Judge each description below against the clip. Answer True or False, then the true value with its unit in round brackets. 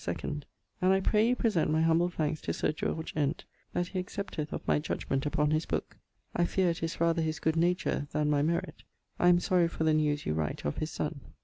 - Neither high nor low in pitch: True (160 Hz)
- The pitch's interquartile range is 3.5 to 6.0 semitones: False (2.8 semitones)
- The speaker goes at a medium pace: False (230 wpm)